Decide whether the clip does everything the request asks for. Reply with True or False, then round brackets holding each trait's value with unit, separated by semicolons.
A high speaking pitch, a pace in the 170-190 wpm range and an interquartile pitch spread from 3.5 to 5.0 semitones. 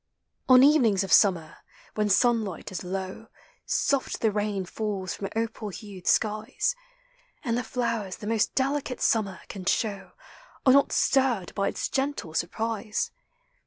False (215 Hz; 140 wpm; 3.9 semitones)